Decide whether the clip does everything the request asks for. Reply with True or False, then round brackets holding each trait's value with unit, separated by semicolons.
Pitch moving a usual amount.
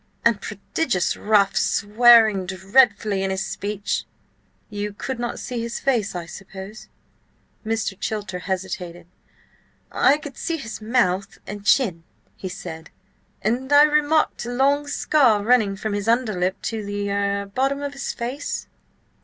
True (4.3 semitones)